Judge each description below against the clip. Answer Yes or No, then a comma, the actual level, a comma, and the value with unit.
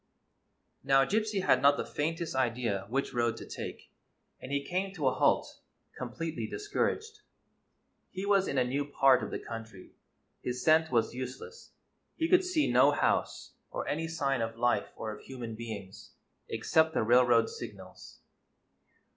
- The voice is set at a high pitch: No, low, 135 Hz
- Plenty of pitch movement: Yes, wide, 5.9 semitones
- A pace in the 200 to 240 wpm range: No, average, 155 wpm